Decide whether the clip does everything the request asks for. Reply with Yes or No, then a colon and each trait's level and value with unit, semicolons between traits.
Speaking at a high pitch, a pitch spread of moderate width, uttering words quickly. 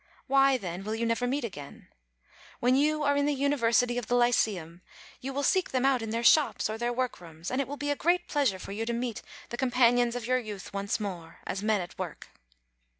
Yes: high, 240 Hz; average, 4.3 semitones; fast, 225 wpm